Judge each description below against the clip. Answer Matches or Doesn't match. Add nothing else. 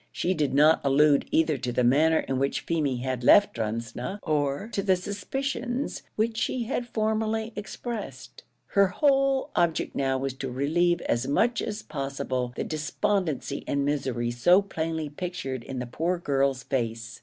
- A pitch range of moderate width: Doesn't match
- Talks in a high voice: Doesn't match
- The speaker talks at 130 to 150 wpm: Doesn't match